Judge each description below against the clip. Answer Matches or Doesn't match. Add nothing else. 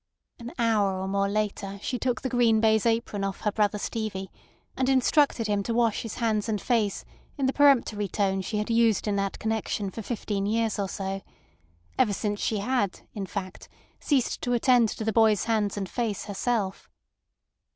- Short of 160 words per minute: Doesn't match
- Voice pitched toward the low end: Doesn't match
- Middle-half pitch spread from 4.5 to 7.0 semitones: Doesn't match